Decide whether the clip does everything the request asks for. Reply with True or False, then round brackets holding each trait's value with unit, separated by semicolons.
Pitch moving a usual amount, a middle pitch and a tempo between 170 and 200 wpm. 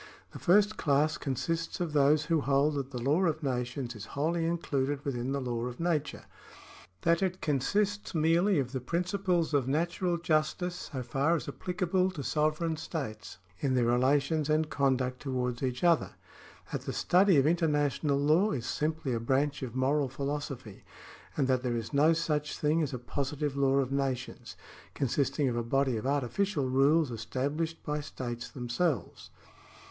True (3.9 semitones; 145 Hz; 175 wpm)